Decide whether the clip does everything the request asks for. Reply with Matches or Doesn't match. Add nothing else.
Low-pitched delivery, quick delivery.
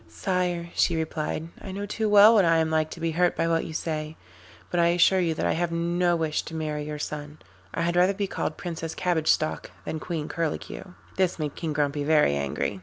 Doesn't match